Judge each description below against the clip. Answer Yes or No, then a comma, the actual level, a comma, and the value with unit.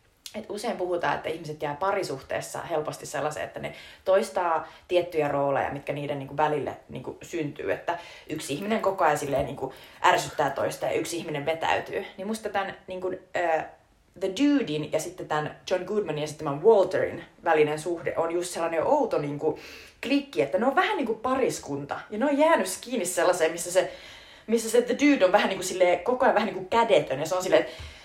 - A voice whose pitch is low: No, medium, 180 Hz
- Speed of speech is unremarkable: No, fast, 190 wpm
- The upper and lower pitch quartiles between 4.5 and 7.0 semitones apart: Yes, wide, 5.6 semitones